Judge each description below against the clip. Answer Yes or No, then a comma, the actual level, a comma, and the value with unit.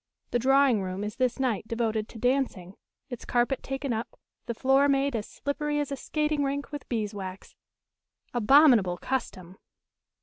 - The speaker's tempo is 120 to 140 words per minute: No, average, 155 wpm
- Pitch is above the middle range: Yes, high, 245 Hz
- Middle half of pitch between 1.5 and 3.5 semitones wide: No, average, 4.5 semitones